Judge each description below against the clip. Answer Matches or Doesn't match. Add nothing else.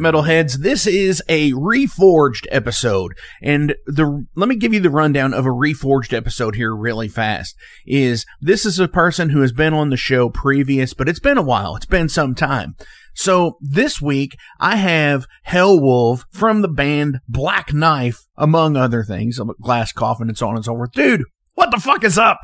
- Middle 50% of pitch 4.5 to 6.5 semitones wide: Matches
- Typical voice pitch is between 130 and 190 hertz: Matches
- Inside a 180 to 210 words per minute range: Matches